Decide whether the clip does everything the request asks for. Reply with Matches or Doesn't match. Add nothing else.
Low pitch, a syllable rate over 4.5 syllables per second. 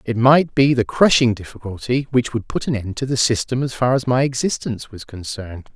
Matches